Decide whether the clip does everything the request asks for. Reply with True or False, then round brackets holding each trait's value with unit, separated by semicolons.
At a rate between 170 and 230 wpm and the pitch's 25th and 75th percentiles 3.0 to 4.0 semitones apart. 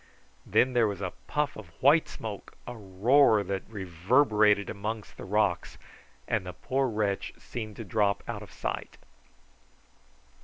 False (145 wpm; 3.4 semitones)